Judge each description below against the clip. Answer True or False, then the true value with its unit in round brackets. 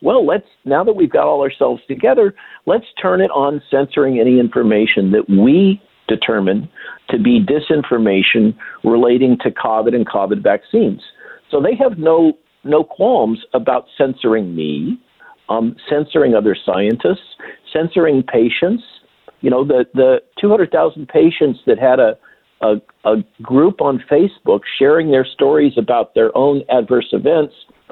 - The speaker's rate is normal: True (145 wpm)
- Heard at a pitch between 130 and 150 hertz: True (140 Hz)